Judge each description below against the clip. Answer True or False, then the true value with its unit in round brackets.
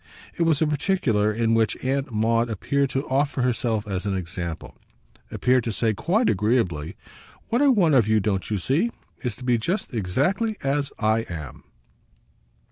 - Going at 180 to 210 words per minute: False (170 wpm)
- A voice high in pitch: False (120 Hz)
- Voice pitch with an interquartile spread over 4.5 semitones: True (5.1 semitones)